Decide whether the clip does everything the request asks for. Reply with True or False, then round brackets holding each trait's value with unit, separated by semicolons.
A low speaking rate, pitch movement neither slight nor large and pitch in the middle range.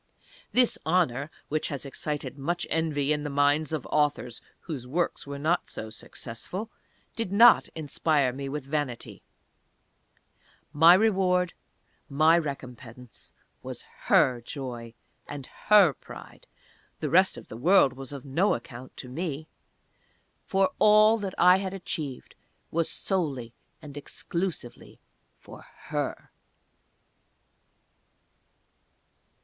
True (115 wpm; 4.9 semitones; 150 Hz)